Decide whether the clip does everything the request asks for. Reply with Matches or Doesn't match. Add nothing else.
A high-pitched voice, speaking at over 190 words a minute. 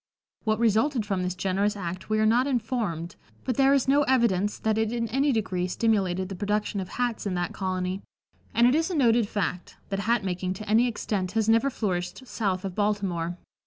Matches